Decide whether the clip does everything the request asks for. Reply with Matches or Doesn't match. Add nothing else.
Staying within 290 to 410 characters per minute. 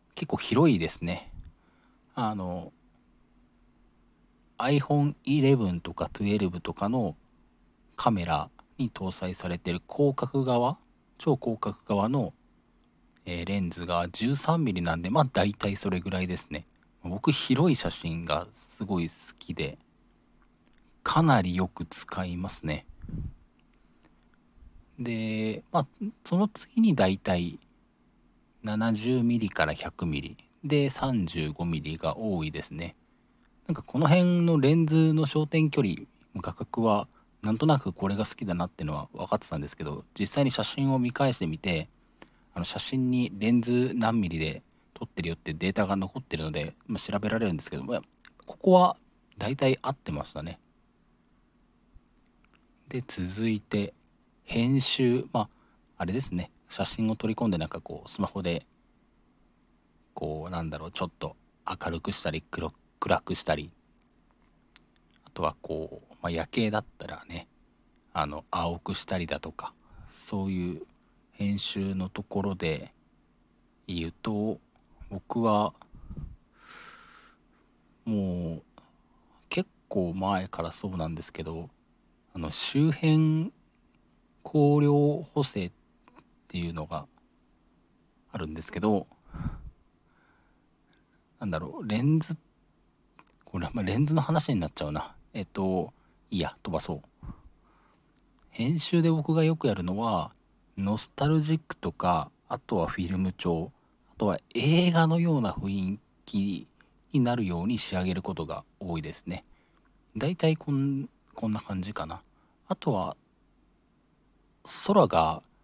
Doesn't match